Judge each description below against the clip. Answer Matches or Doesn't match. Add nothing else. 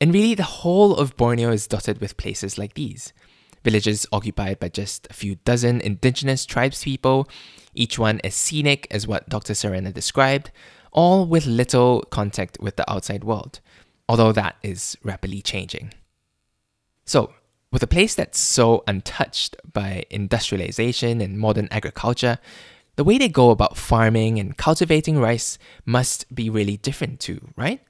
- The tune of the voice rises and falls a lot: Doesn't match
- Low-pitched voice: Matches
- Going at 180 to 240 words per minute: Doesn't match